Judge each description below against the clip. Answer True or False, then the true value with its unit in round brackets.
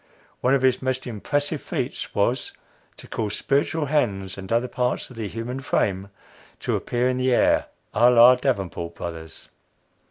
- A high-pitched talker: False (125 Hz)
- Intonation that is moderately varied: True (4.6 semitones)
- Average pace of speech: True (160 wpm)